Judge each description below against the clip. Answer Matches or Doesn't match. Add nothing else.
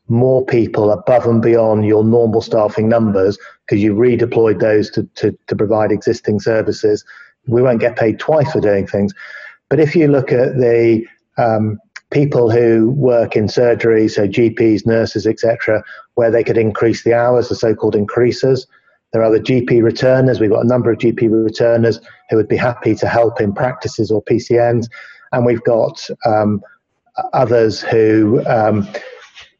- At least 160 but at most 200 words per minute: Matches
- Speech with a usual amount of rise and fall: Doesn't match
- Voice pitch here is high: Doesn't match